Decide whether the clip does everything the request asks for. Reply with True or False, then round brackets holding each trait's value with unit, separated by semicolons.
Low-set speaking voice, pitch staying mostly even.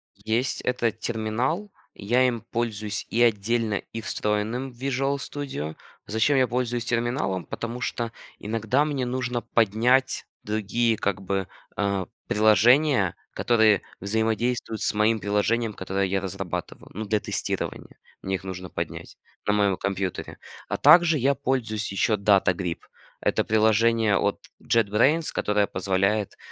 False (110 Hz; 3.2 semitones)